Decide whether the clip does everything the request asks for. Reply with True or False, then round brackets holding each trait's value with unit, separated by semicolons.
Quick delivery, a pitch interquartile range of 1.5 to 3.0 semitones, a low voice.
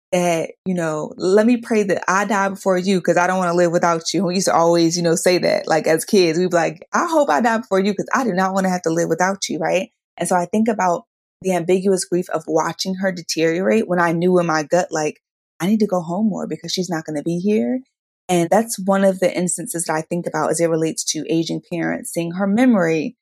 False (265 wpm; 2.7 semitones; 180 Hz)